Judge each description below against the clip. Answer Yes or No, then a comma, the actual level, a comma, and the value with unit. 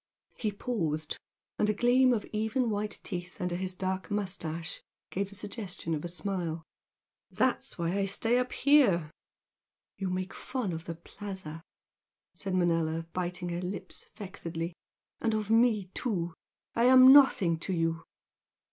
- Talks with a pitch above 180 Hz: Yes, high, 190 Hz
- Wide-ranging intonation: No, average, 4.1 semitones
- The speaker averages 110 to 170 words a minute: Yes, average, 145 wpm